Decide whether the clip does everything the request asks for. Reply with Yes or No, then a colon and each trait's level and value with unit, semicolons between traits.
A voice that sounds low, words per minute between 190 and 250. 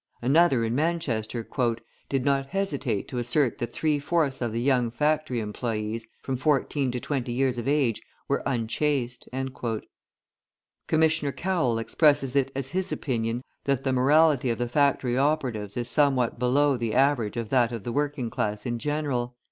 No: low, 130 Hz; average, 165 wpm